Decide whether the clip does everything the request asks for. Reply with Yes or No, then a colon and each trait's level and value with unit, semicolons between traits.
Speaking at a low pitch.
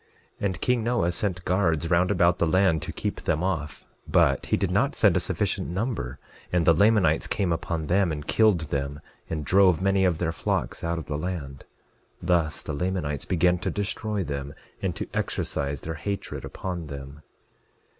Yes: very low, 85 Hz